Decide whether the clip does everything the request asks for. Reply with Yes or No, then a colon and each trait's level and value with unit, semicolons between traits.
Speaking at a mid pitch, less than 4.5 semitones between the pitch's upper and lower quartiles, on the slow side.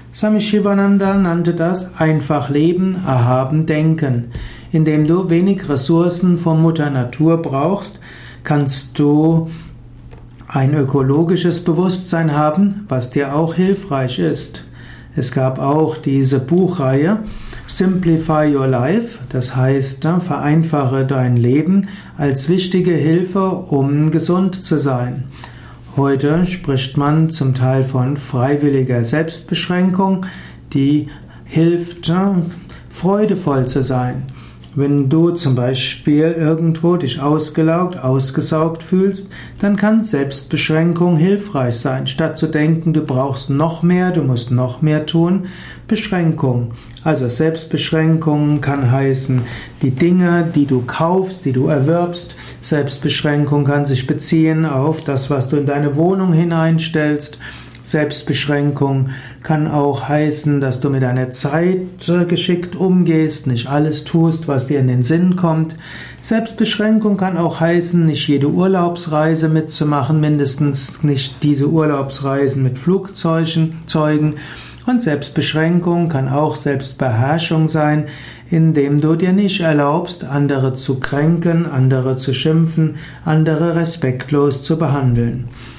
Yes: medium, 155 Hz; average, 3.7 semitones; slow, 115 wpm